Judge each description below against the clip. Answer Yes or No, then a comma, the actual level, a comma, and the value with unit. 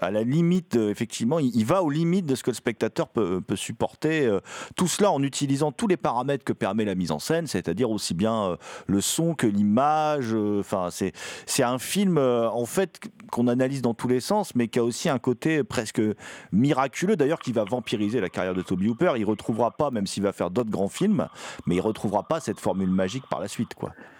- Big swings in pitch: Yes, wide, 5.9 semitones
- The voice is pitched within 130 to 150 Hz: No, low, 120 Hz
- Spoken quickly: Yes, fast, 230 wpm